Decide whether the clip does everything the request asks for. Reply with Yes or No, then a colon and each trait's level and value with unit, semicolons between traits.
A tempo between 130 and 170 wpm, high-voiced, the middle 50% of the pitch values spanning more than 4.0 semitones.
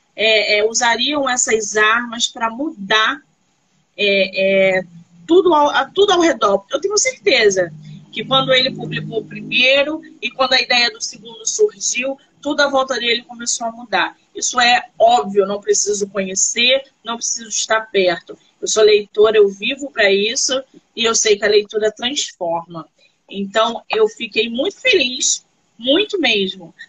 Yes: average, 150 wpm; high, 225 Hz; average, 4.6 semitones